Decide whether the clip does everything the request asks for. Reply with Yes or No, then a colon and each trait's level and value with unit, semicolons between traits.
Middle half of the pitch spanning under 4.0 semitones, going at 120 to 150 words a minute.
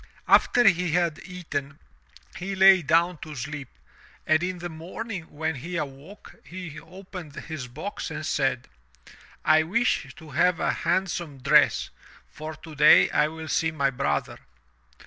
Yes: average, 3.5 semitones; average, 145 wpm